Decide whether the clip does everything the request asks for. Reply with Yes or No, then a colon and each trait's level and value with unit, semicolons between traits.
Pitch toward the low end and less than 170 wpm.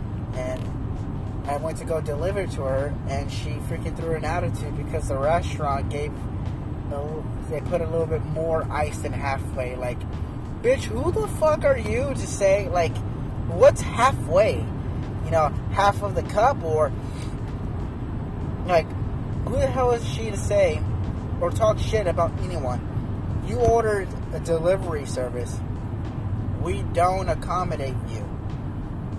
Yes: low, 110 Hz; average, 140 wpm